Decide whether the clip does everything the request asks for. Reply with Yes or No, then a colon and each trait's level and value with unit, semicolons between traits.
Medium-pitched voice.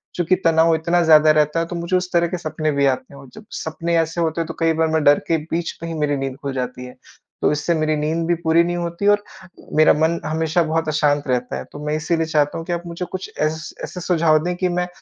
Yes: medium, 160 Hz